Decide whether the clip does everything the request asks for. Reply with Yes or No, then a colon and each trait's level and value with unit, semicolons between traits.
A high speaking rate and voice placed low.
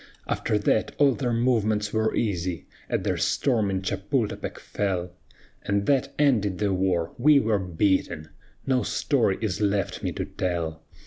No: average, 145 wpm; low, 105 Hz